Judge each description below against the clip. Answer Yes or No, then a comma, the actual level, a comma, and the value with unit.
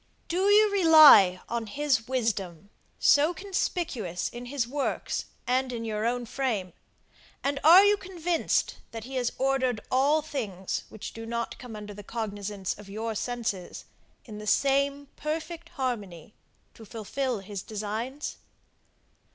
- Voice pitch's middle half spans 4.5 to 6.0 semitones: Yes, average, 5.3 semitones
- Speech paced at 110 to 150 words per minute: Yes, average, 140 wpm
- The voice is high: Yes, high, 245 Hz